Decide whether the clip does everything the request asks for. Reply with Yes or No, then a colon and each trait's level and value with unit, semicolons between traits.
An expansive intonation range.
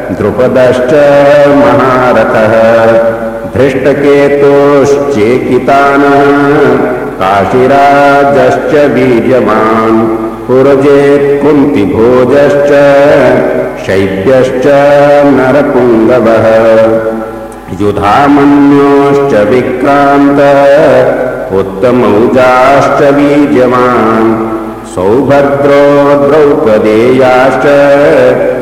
No: average, 4.1 semitones